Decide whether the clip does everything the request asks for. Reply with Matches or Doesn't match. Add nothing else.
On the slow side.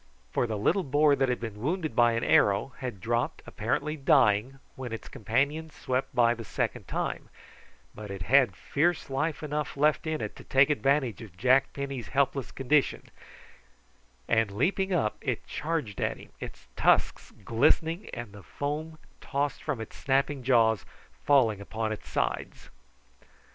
Doesn't match